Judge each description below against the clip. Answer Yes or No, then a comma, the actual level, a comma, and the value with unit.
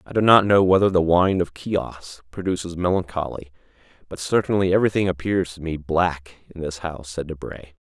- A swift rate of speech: No, average, 175 wpm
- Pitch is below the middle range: Yes, very low, 85 Hz